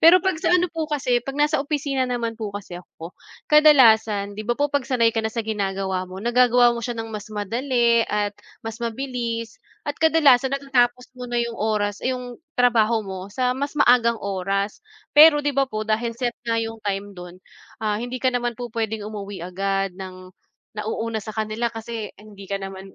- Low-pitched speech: No, high, 230 Hz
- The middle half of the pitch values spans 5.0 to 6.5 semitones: No, average, 3.5 semitones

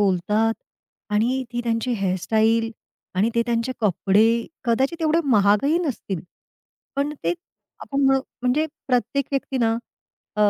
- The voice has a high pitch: Yes, high, 230 Hz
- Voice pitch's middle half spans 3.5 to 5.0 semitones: Yes, average, 4.0 semitones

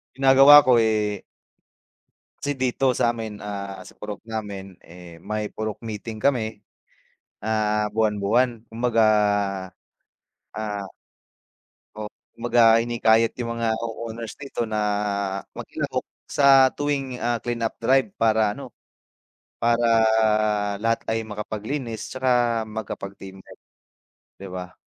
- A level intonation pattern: Yes, narrow, 2.2 semitones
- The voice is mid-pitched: No, low, 110 Hz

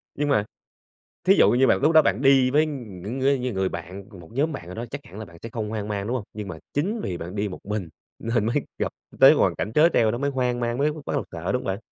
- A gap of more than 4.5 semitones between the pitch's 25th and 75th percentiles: Yes, wide, 5.5 semitones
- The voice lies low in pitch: Yes, low, 115 Hz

